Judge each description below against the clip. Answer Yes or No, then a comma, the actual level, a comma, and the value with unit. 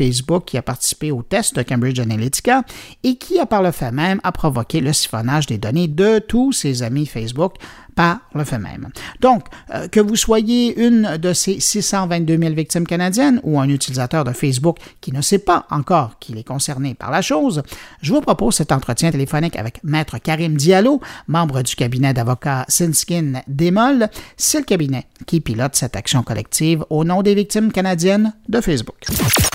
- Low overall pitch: No, medium, 160 Hz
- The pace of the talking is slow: No, average, 180 wpm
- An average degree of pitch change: No, wide, 7.0 semitones